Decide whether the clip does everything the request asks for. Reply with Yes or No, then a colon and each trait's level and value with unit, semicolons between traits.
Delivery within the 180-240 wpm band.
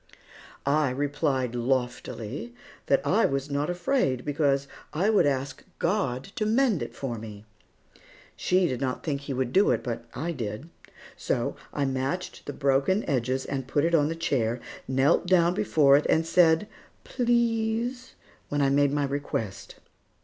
No: average, 155 wpm